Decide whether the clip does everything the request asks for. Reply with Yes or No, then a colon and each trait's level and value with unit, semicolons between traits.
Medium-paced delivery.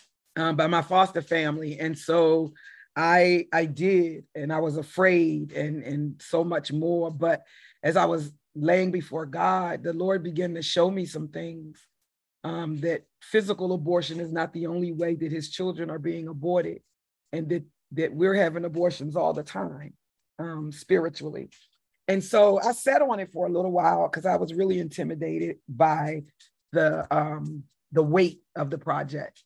Yes: average, 170 wpm